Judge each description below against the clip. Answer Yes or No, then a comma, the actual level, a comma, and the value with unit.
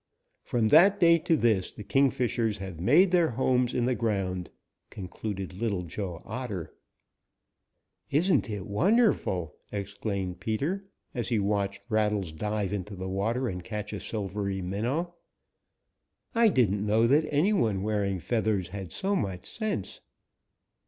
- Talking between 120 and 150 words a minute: Yes, average, 140 wpm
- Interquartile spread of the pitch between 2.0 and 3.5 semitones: No, average, 4.8 semitones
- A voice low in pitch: Yes, low, 105 Hz